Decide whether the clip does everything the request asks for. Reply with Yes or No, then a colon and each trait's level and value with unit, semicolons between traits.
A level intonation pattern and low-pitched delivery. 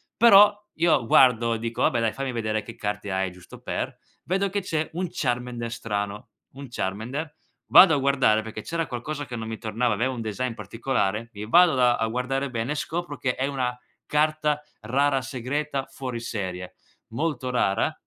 No: average, 4.4 semitones; low, 125 Hz